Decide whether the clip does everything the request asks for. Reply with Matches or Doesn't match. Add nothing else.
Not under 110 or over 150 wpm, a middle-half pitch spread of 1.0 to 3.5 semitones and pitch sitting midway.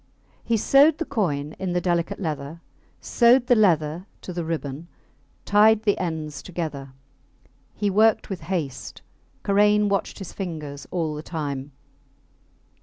Doesn't match